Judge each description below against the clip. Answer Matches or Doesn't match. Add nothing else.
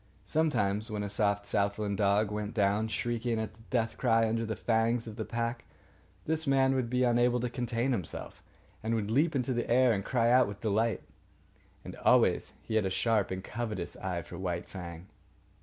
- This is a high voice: Doesn't match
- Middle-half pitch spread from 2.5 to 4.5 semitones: Matches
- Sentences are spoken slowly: Doesn't match